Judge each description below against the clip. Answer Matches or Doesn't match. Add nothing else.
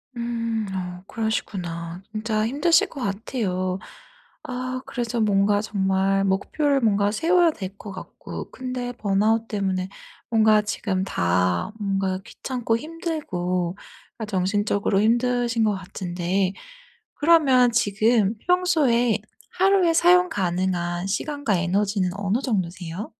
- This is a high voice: Matches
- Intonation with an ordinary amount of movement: Matches